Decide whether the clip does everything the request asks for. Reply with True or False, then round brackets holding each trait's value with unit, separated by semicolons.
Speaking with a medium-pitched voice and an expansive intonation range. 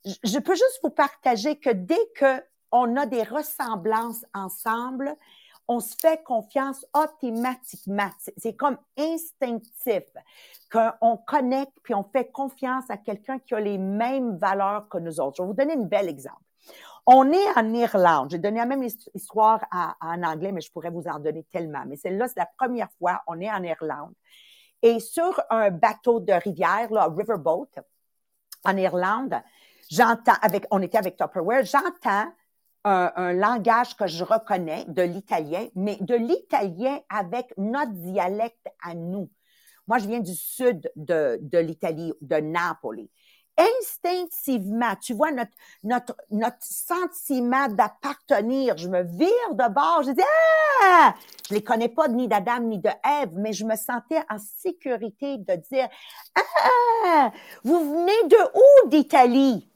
False (235 Hz; 6.2 semitones)